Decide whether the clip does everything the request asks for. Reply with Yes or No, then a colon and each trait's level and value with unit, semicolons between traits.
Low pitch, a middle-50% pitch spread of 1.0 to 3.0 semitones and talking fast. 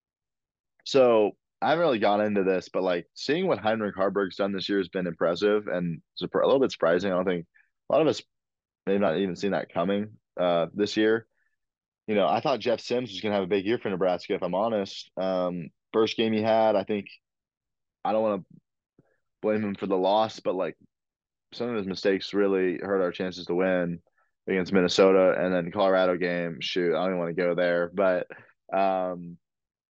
Yes: very low, 95 Hz; narrow, 2.4 semitones; fast, 210 wpm